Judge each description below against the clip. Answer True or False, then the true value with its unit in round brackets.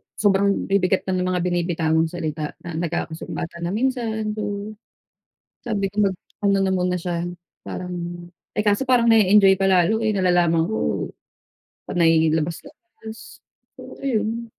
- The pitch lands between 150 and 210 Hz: True (190 Hz)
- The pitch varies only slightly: False (3.8 semitones)